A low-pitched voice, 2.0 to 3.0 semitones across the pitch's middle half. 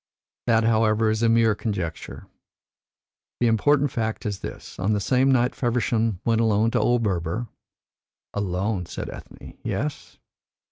Yes: low, 110 Hz; narrow, 2.6 semitones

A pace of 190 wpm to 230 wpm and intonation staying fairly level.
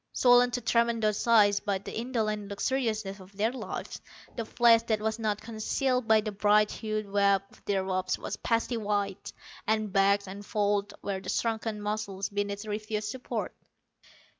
No: average, 165 wpm; narrow, 2.0 semitones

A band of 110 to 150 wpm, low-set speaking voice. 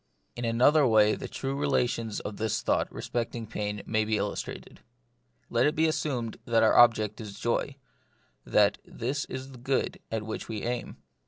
No: average, 170 wpm; low, 115 Hz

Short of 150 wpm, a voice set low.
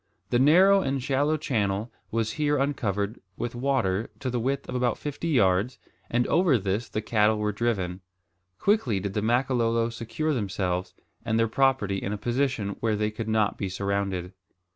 No: average, 170 wpm; low, 115 Hz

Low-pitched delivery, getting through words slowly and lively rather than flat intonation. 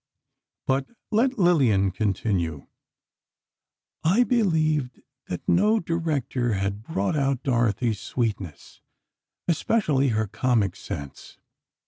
Yes: low, 125 Hz; slow, 90 wpm; wide, 8.0 semitones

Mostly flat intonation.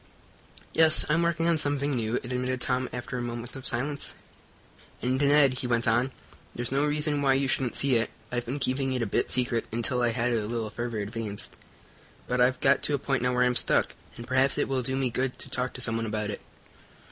Yes: narrow, 2.3 semitones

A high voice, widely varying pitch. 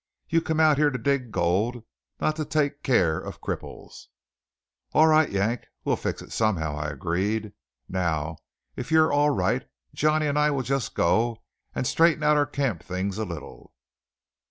No: low, 120 Hz; wide, 8.2 semitones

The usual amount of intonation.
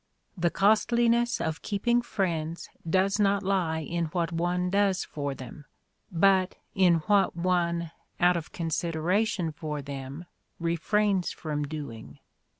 Yes: average, 3.6 semitones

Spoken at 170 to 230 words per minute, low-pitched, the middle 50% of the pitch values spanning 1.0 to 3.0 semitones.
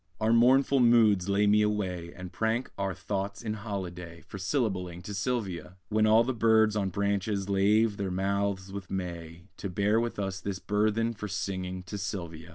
Yes: average, 175 wpm; low, 100 Hz; average, 2.7 semitones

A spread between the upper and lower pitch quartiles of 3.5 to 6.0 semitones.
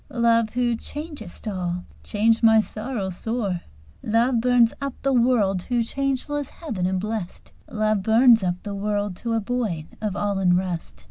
Yes: average, 4.0 semitones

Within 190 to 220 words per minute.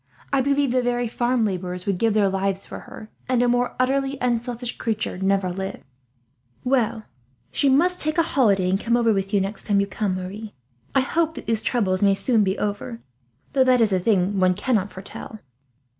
Yes: average, 200 wpm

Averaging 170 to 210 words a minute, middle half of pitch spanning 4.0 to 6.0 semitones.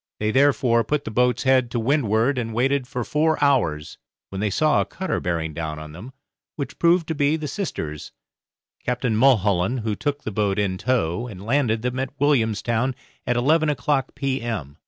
Yes: average, 180 wpm; average, 5.0 semitones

